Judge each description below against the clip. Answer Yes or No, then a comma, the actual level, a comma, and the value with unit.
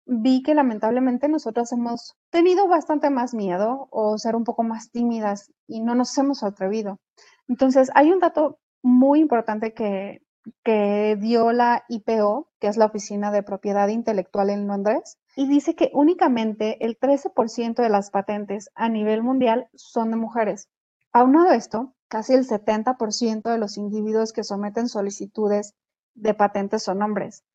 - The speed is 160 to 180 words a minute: No, average, 150 wpm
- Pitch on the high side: Yes, high, 230 Hz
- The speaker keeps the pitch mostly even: No, average, 3.4 semitones